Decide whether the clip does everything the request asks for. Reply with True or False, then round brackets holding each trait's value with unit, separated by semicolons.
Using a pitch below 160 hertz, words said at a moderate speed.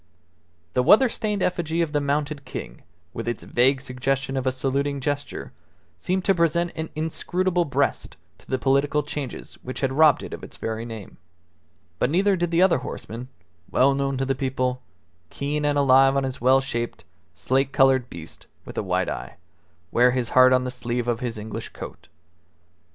True (135 Hz; 180 wpm)